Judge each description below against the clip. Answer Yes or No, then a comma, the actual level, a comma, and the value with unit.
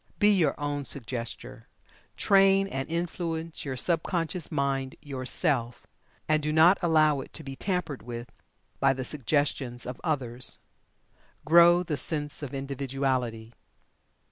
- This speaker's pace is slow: Yes, slow, 130 wpm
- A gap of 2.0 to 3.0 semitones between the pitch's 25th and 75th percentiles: No, average, 4.0 semitones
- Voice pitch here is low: No, medium, 145 Hz